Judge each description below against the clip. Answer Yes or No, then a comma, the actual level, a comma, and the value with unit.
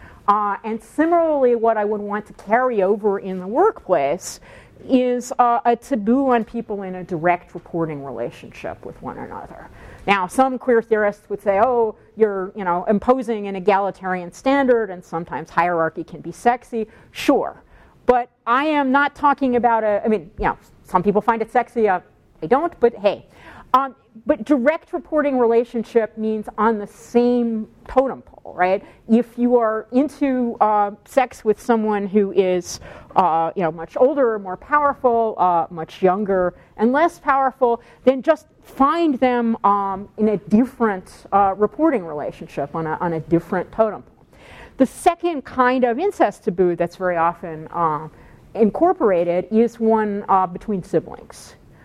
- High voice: Yes, high, 220 Hz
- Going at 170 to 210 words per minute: No, average, 160 wpm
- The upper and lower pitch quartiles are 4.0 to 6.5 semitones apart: Yes, average, 4.7 semitones